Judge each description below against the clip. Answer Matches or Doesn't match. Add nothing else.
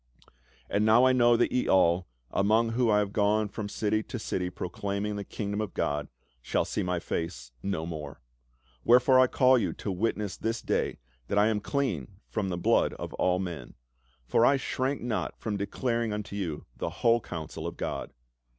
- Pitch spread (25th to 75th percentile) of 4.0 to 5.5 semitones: Matches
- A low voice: Matches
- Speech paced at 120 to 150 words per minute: Doesn't match